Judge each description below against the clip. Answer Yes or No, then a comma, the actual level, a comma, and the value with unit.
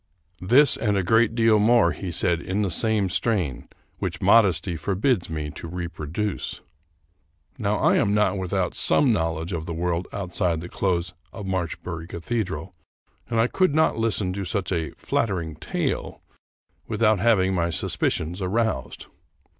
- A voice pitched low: Yes, very low, 95 Hz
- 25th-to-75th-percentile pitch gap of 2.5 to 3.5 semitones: No, average, 4.1 semitones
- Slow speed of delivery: No, average, 165 wpm